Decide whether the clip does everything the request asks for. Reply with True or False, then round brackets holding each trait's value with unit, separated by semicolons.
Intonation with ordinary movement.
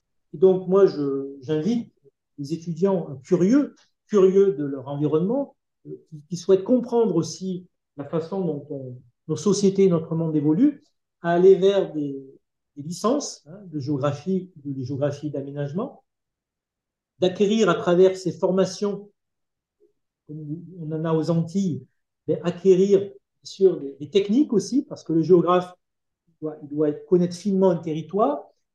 True (4.3 semitones)